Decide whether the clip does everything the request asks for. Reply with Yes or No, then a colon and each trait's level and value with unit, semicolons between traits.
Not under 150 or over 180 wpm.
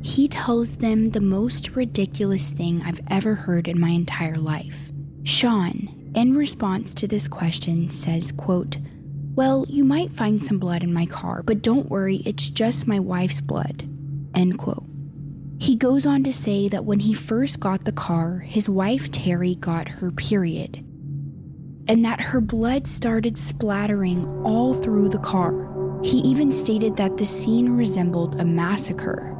Yes: average, 160 wpm